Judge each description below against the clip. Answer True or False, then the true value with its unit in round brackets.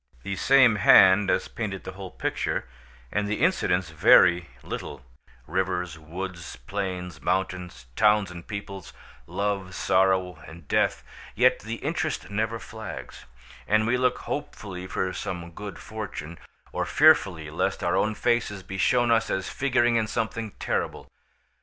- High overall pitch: False (95 Hz)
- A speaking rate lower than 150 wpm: True (140 wpm)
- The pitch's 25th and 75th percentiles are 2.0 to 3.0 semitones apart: False (3.6 semitones)